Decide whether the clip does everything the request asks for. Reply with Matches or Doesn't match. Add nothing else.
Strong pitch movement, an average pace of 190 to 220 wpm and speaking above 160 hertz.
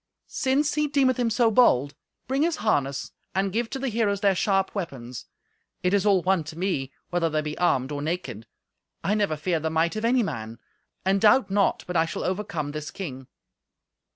Matches